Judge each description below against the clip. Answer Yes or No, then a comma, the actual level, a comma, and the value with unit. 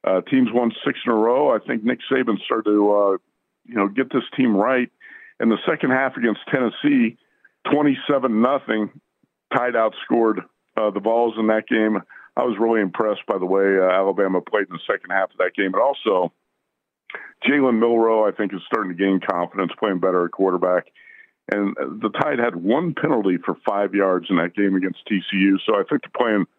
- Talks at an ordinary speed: Yes, average, 195 wpm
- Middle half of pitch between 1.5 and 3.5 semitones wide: No, average, 4.1 semitones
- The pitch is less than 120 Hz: Yes, low, 105 Hz